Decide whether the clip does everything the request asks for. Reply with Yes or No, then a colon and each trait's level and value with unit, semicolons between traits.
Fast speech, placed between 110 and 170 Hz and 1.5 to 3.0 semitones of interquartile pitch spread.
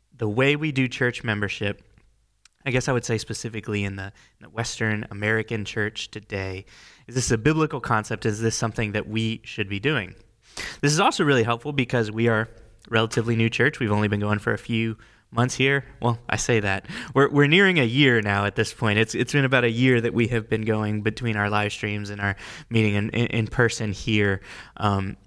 Yes: fast, 215 wpm; low, 115 Hz; narrow, 2.6 semitones